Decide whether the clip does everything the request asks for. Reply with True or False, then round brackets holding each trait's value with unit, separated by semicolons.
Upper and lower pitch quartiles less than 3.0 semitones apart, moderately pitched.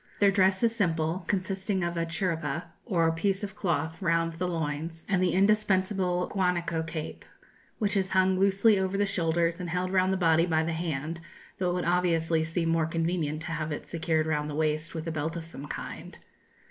True (2.6 semitones; 170 Hz)